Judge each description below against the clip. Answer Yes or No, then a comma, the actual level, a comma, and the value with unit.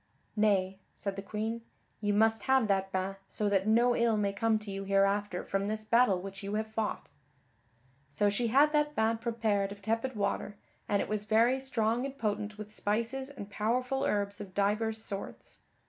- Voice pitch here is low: No, high, 215 Hz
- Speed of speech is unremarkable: Yes, average, 185 wpm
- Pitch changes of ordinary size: No, narrow, 2.3 semitones